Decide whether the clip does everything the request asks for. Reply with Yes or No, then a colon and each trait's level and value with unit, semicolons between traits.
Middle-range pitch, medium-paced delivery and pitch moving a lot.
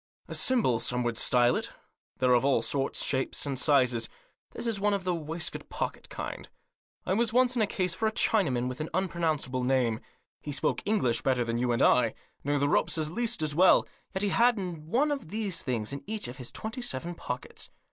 No: medium, 155 Hz; fast, 215 wpm; wide, 8.1 semitones